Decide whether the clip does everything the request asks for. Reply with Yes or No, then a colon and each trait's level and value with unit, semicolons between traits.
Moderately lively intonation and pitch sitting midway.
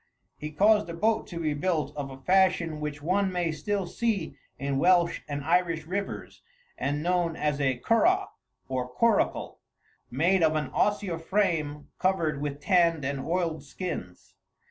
Yes: average, 4.2 semitones; medium, 165 Hz